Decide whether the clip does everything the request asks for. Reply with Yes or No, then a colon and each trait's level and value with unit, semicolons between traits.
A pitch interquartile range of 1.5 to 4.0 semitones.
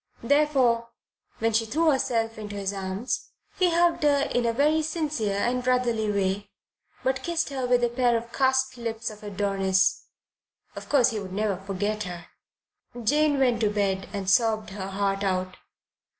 No: average, 4.6 semitones